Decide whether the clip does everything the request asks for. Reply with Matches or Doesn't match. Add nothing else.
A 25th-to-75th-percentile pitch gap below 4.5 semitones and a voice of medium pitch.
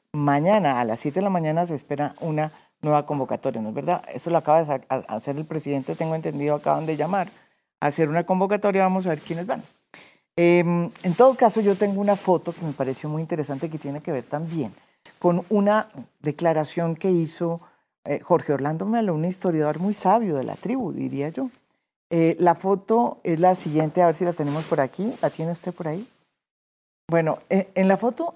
Matches